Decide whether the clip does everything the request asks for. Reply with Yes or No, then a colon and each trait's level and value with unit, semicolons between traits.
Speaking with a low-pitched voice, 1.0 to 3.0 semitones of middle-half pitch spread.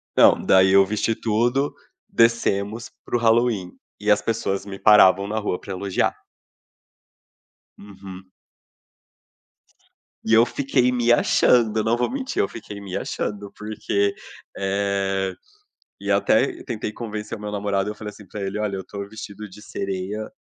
Yes: low, 105 Hz; narrow, 2.5 semitones